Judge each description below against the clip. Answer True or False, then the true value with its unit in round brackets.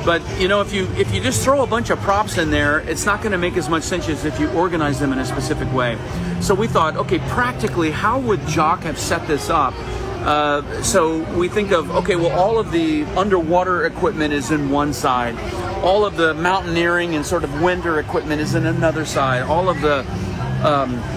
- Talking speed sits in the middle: False (220 wpm)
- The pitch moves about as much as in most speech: True (3.6 semitones)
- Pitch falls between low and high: True (160 Hz)